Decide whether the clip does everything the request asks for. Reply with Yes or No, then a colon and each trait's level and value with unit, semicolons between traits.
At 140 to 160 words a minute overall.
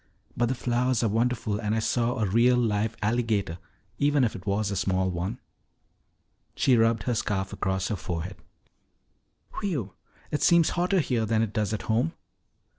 No: average, 170 wpm